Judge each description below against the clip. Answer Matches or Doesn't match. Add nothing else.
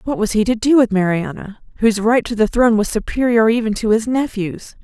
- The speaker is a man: Doesn't match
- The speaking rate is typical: Doesn't match